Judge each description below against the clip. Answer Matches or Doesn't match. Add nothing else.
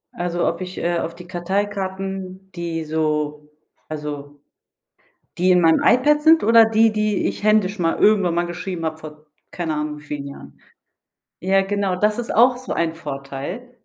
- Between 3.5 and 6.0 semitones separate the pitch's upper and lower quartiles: Matches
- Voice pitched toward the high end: Doesn't match